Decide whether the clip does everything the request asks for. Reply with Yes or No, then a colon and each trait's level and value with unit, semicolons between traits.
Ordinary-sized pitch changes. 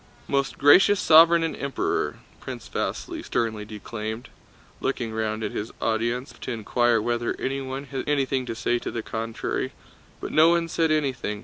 Yes: average, 4.0 semitones